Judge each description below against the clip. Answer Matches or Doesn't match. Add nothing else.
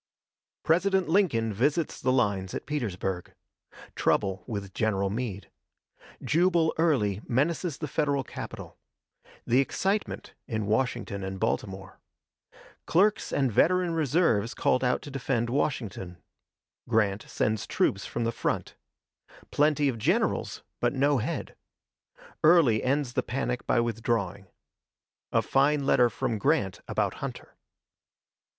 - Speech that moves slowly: Matches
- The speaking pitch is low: Matches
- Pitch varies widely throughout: Matches